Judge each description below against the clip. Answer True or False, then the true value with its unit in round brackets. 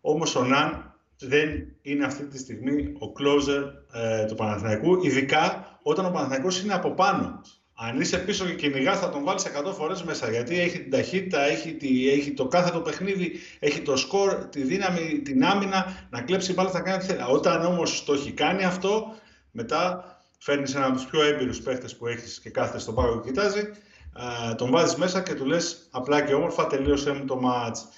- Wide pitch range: True (5.8 semitones)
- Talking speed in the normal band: False (195 wpm)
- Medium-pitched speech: True (145 Hz)